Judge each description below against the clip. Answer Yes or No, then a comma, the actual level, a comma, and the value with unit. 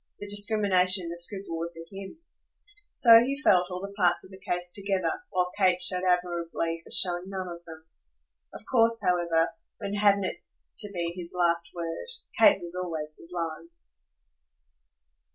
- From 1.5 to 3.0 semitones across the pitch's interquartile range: Yes, average, 2.7 semitones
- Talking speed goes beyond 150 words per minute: Yes, average, 165 wpm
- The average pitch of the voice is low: No, medium, 180 Hz